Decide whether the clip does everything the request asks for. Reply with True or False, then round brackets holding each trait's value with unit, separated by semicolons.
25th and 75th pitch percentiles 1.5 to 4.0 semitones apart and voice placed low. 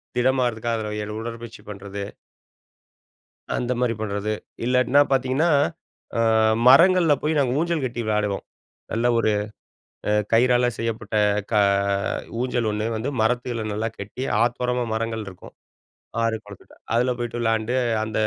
True (2.4 semitones; 115 Hz)